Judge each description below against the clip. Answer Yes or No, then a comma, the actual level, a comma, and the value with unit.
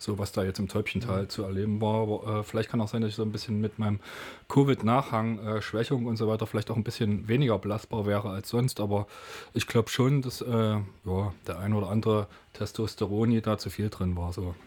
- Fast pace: Yes, fast, 225 wpm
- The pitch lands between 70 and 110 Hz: Yes, low, 105 Hz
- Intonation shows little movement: Yes, narrow, 1.7 semitones